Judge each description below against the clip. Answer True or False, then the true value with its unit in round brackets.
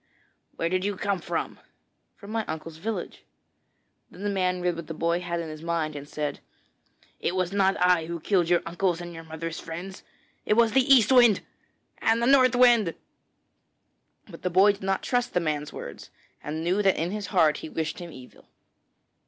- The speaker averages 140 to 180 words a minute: False (195 wpm)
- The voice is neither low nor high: True (180 Hz)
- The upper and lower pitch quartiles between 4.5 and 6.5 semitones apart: False (3.8 semitones)